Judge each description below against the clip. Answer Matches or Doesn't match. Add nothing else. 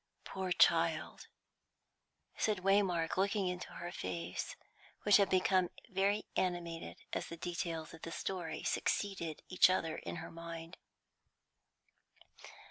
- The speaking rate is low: Matches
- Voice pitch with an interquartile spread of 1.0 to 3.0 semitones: Matches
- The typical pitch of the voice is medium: Matches